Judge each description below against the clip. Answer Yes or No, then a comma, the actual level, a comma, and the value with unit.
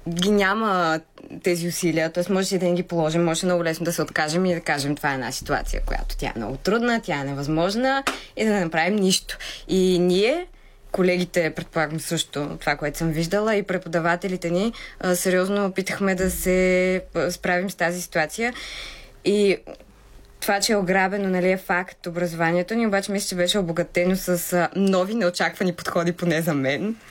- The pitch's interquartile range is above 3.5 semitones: No, narrow, 2.4 semitones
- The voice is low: No, medium, 180 Hz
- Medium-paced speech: No, fast, 175 wpm